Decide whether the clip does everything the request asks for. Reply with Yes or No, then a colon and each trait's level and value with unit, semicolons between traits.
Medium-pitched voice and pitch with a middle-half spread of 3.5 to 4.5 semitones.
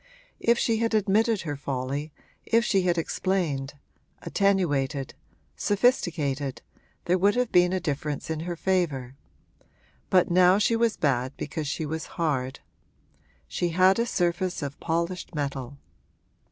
No: medium, 170 Hz; average, 5.1 semitones